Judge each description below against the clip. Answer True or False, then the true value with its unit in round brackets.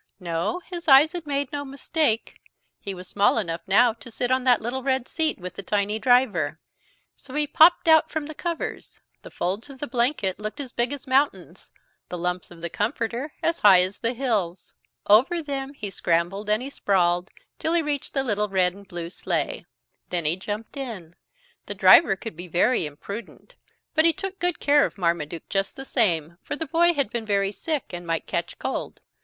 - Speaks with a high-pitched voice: True (230 Hz)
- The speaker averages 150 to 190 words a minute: False (200 wpm)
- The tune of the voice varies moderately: False (7.4 semitones)